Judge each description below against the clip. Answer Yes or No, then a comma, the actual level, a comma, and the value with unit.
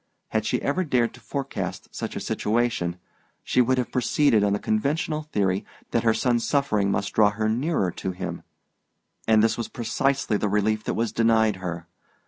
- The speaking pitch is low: Yes, low, 110 Hz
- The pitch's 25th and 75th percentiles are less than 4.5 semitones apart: Yes, average, 3.7 semitones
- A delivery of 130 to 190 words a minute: Yes, average, 180 wpm